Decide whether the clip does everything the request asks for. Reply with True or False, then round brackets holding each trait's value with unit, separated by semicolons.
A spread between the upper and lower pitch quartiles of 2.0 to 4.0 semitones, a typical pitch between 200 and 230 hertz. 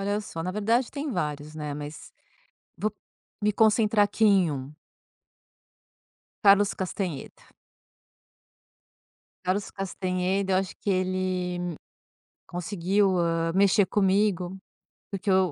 False (2.4 semitones; 190 Hz)